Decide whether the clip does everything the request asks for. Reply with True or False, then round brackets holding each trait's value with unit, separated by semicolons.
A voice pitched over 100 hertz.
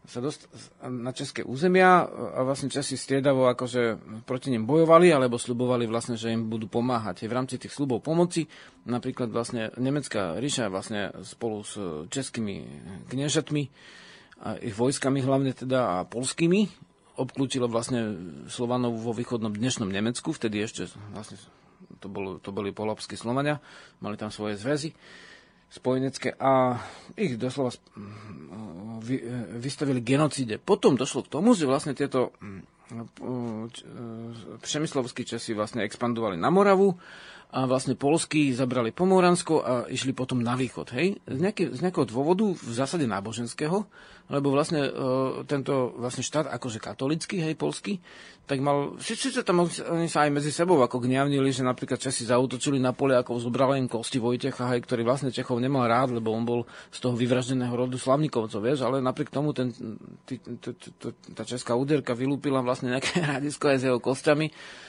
True (130 Hz)